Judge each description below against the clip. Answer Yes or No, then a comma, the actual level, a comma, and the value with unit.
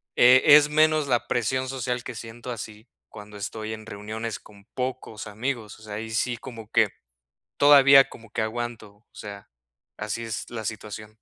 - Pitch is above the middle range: No, low, 115 Hz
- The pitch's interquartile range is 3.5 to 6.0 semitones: No, average, 2.8 semitones